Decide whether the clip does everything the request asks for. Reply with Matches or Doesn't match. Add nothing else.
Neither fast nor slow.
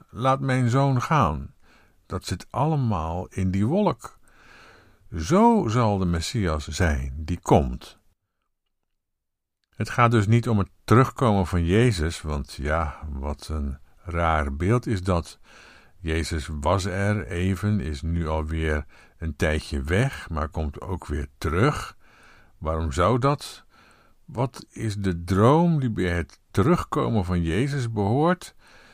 Doesn't match